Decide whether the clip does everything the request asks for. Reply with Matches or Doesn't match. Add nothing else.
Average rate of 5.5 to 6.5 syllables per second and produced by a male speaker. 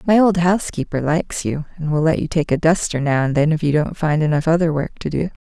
Doesn't match